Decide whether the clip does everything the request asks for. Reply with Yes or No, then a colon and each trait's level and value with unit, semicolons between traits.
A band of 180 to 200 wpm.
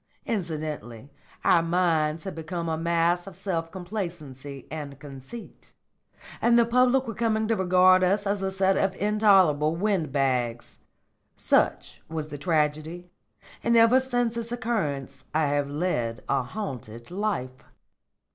No: slow, 135 wpm